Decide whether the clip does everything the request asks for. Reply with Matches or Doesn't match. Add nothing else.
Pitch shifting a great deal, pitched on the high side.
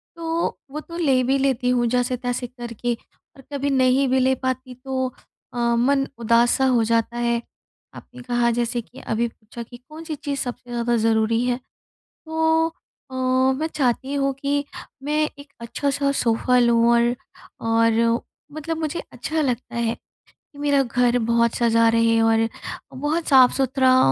Doesn't match